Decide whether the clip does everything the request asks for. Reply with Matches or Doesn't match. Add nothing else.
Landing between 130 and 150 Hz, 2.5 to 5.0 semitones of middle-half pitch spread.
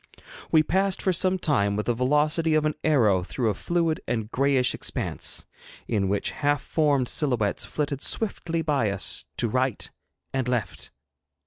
Doesn't match